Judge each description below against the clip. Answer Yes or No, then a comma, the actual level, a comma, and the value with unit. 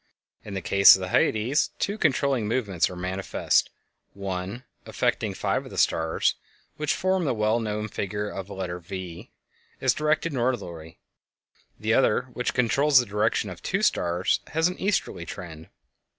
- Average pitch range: No, wide, 5.9 semitones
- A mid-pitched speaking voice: No, low, 105 Hz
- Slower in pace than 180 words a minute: Yes, average, 160 wpm